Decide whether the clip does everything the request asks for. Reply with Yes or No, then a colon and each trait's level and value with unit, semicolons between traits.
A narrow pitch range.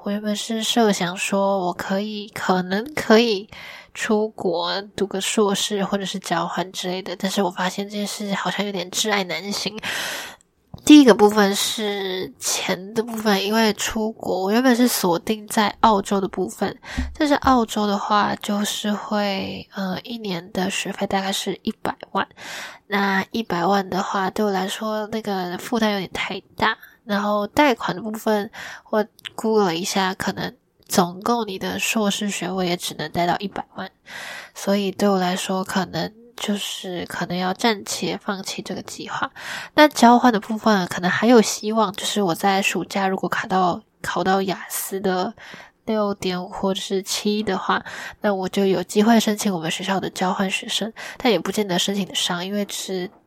Yes: narrow, 2.3 semitones